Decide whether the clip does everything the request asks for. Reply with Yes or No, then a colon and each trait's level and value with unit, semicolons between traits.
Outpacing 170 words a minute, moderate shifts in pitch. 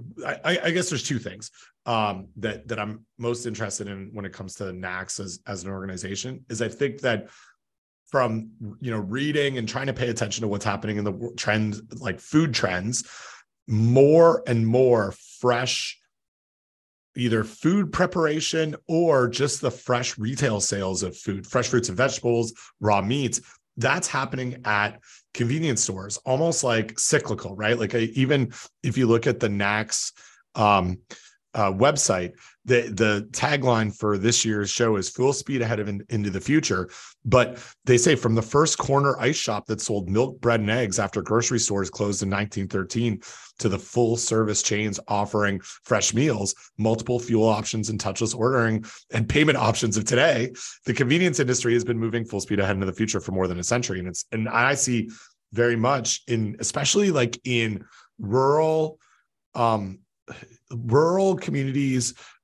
No: average, 165 wpm; average, 3.3 semitones